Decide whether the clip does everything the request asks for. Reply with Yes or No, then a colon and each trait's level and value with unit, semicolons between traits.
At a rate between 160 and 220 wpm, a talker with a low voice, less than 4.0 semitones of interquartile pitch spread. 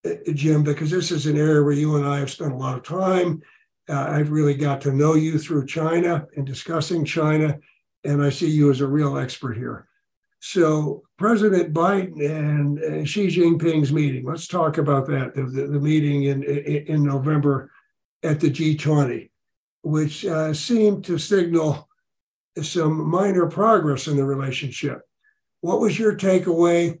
No: average, 165 wpm; medium, 155 Hz; average, 3.0 semitones